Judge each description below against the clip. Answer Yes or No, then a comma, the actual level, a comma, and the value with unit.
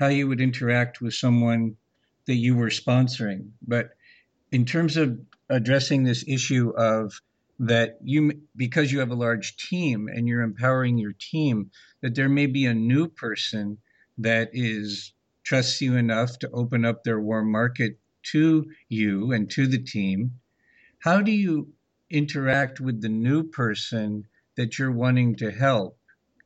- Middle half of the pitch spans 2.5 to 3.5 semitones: Yes, average, 3.0 semitones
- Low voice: Yes, low, 120 Hz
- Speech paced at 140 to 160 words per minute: Yes, average, 155 wpm